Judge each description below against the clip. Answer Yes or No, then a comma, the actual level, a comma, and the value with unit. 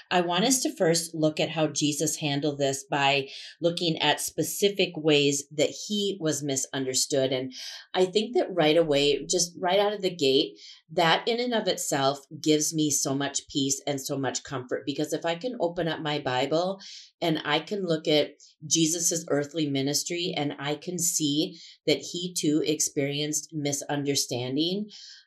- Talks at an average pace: Yes, average, 170 wpm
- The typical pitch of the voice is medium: Yes, medium, 155 Hz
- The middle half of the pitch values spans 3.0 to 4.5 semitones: Yes, average, 3.3 semitones